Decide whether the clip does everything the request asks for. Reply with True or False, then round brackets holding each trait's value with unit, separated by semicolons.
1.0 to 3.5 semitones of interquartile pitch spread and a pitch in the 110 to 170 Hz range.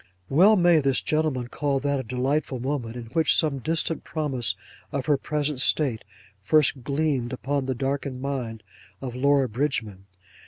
True (2.9 semitones; 140 Hz)